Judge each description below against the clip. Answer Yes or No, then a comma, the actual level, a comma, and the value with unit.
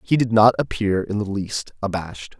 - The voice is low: Yes, low, 105 Hz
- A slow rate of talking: No, average, 200 wpm